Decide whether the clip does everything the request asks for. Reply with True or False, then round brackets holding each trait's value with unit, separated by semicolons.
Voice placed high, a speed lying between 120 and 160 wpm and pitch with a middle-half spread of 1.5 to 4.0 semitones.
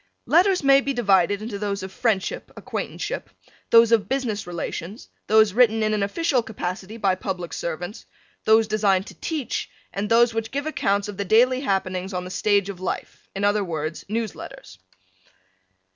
False (210 Hz; 170 wpm; 3.3 semitones)